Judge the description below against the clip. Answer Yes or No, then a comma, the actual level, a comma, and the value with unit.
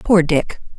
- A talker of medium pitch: Yes, medium, 170 Hz